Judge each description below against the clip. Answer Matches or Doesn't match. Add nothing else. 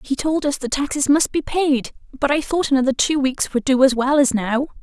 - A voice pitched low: Doesn't match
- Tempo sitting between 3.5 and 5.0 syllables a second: Doesn't match